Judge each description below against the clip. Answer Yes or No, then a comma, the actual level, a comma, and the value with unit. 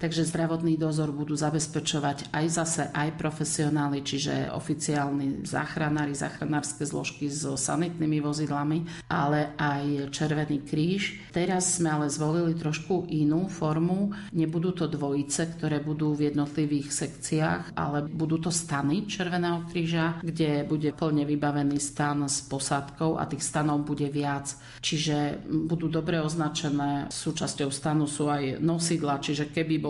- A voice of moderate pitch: Yes, medium, 150 Hz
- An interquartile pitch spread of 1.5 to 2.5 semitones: Yes, narrow, 2.0 semitones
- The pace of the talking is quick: No, average, 130 wpm